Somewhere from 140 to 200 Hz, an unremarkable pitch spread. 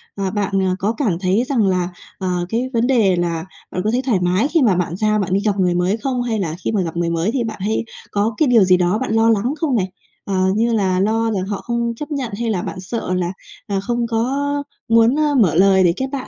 No: high, 210 Hz; average, 4.3 semitones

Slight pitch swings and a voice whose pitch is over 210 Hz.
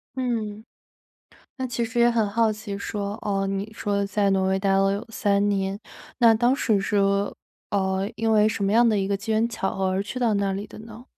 No: narrow, 2.3 semitones; high, 205 Hz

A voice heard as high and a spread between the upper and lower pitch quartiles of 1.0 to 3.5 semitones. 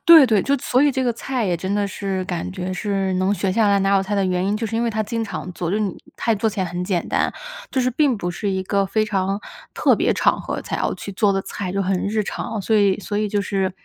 Yes: high, 200 Hz; average, 2.7 semitones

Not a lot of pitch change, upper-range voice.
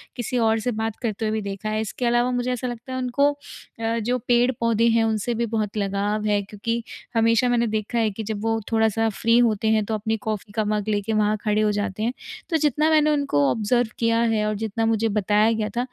Yes: narrow, 2.0 semitones; high, 225 Hz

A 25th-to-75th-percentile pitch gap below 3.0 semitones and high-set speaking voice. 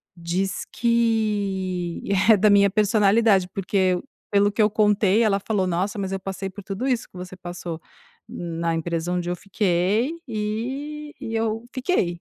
No: average, 3.3 semitones; high, 200 Hz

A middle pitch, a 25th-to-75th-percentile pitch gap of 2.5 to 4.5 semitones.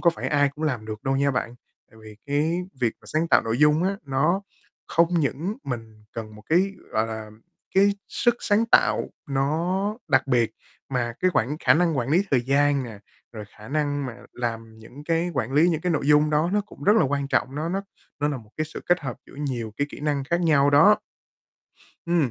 No: medium, 145 Hz; average, 5.1 semitones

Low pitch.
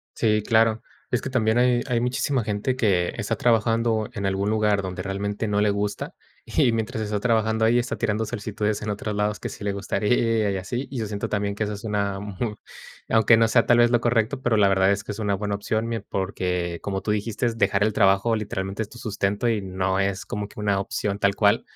Yes: low, 105 Hz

